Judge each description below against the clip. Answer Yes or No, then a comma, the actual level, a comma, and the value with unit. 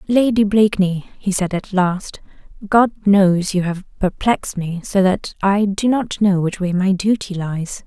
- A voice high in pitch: Yes, high, 195 Hz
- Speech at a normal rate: Yes, average, 175 wpm